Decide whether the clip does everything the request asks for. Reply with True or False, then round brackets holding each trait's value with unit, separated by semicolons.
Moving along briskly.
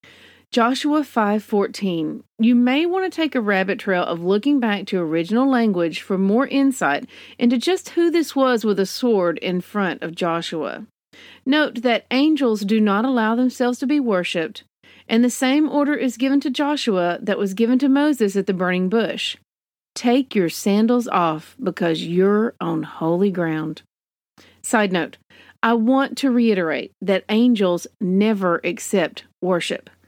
False (155 wpm)